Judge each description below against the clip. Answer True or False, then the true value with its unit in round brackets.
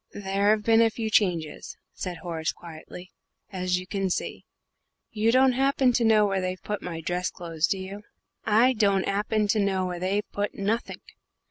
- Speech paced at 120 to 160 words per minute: False (180 wpm)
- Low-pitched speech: False (200 Hz)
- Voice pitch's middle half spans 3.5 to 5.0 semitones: False (3.0 semitones)